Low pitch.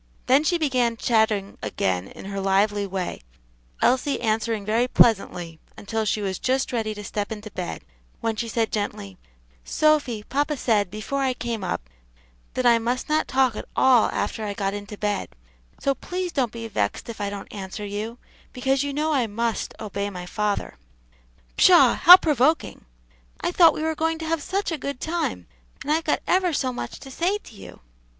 No: high, 230 Hz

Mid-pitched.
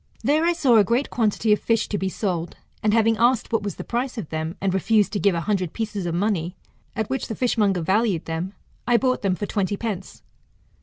No: high, 210 Hz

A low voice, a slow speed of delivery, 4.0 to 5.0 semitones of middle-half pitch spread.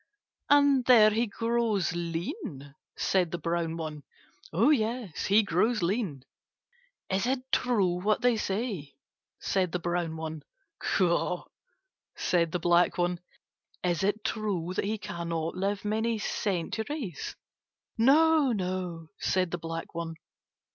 No: medium, 185 Hz; slow, 125 wpm; average, 4.7 semitones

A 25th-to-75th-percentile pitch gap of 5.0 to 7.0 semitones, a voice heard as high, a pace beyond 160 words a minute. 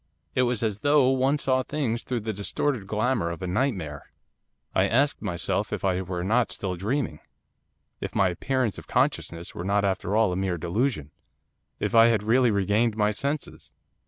No: average, 5.3 semitones; low, 110 Hz; average, 180 wpm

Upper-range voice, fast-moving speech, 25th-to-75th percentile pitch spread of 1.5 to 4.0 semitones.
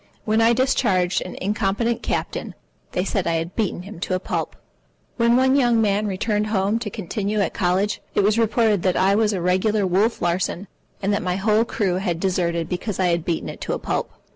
Yes: high, 200 Hz; fast, 210 wpm; average, 3.2 semitones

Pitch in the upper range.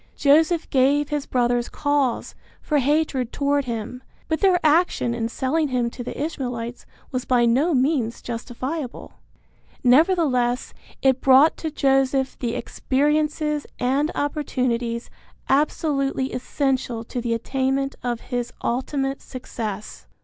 Yes: very high, 265 Hz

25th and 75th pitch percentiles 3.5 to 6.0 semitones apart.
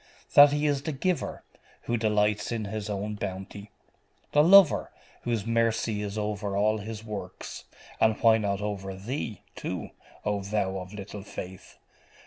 No: narrow, 2.4 semitones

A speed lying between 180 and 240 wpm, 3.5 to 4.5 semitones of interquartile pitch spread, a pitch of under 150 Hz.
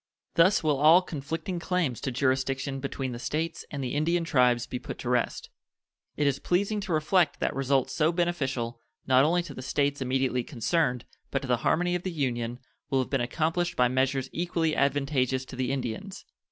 Yes: average, 190 wpm; average, 4.2 semitones; medium, 140 Hz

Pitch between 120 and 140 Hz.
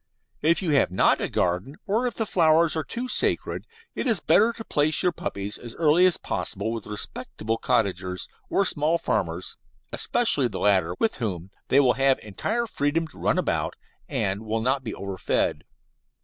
Yes: low, 135 Hz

